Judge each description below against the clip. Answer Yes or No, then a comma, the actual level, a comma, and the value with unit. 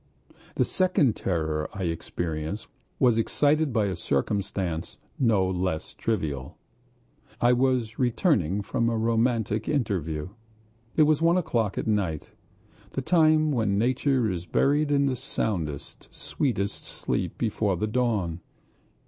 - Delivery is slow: Yes, slow, 125 wpm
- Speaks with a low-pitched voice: Yes, low, 110 Hz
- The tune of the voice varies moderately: No, wide, 6.1 semitones